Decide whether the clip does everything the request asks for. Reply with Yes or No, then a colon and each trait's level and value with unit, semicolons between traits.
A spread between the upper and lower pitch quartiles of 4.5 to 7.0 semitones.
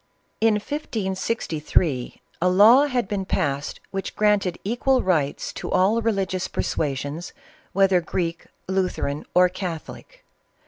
No: average, 4.1 semitones